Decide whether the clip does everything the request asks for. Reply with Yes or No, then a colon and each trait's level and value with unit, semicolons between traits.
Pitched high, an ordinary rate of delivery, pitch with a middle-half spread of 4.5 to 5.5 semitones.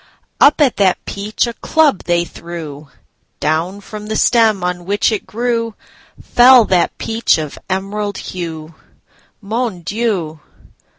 No: high, 200 Hz; slow, 115 wpm; average, 4.8 semitones